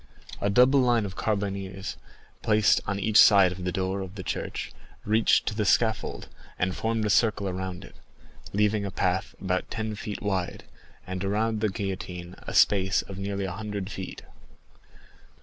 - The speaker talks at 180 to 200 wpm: No, average, 165 wpm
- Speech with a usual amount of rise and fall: No, narrow, 2.2 semitones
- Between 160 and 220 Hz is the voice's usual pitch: No, low, 100 Hz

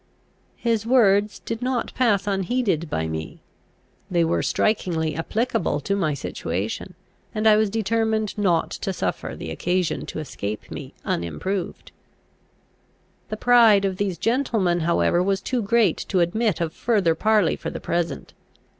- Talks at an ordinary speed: Yes, average, 145 wpm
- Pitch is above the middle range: Yes, high, 195 Hz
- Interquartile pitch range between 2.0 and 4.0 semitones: No, average, 4.7 semitones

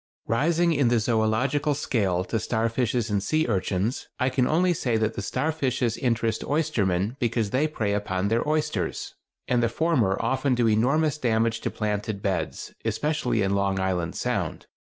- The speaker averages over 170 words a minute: No, average, 160 wpm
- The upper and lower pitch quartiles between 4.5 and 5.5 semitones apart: Yes, average, 5.1 semitones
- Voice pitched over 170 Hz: No, low, 115 Hz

